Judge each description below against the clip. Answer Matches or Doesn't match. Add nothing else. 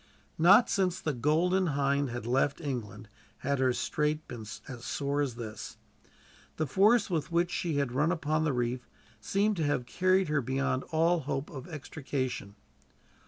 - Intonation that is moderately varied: Matches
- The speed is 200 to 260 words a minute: Doesn't match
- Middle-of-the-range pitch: Matches